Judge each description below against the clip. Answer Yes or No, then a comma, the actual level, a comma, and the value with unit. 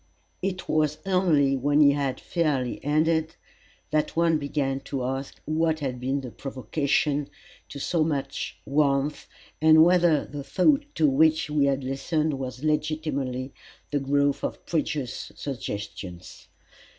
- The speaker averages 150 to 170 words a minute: No, slow, 135 wpm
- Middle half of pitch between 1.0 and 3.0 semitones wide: Yes, narrow, 2.6 semitones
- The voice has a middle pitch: Yes, medium, 145 Hz